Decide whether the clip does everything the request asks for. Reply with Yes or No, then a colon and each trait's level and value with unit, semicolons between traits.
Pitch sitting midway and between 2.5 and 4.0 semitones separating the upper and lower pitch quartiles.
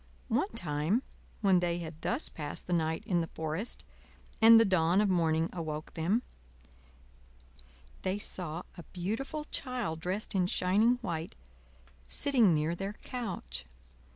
No: medium, 180 Hz; average, 4.9 semitones